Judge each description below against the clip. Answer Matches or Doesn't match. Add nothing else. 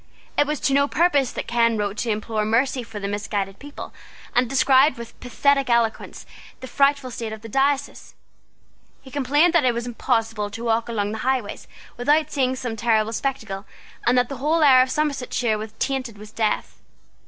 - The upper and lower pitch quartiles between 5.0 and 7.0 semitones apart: Doesn't match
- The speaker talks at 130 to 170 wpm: Doesn't match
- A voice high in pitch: Matches